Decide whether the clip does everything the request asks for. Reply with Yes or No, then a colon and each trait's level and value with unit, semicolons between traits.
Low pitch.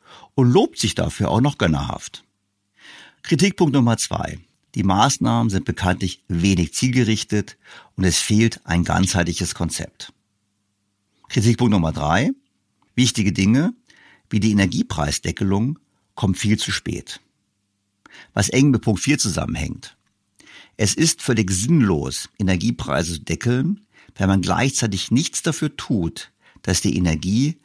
Yes: low, 105 Hz